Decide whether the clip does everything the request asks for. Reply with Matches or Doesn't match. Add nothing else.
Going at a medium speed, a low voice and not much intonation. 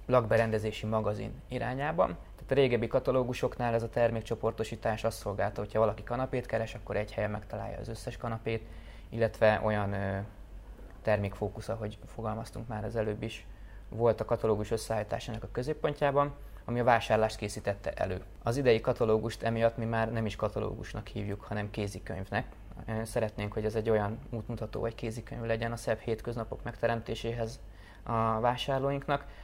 Matches